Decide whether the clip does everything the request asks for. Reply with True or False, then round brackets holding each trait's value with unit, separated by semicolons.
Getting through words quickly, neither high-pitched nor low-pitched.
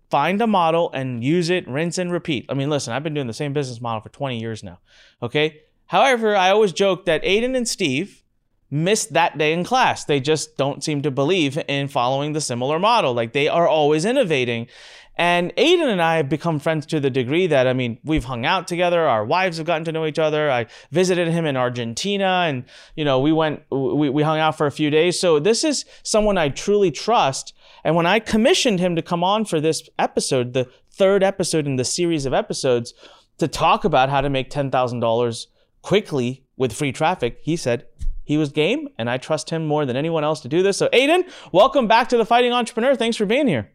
True (220 wpm; 155 Hz)